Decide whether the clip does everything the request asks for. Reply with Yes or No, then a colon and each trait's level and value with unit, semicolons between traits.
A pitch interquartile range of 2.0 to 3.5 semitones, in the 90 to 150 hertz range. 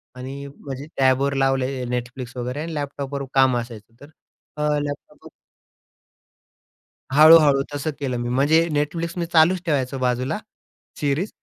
Yes: narrow, 2.6 semitones; medium, 140 Hz